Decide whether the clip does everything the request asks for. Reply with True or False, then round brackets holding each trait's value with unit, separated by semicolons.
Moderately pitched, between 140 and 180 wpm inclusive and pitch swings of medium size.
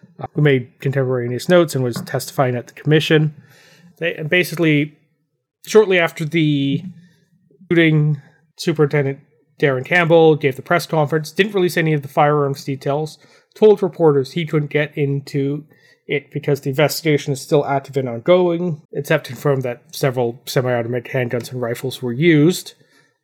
True (150 Hz; 145 wpm; 3.0 semitones)